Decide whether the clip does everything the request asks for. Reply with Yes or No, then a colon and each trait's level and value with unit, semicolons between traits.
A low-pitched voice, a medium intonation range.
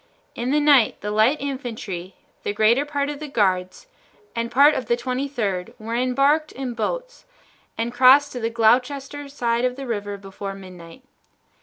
No: high, 245 Hz; average, 4.6 semitones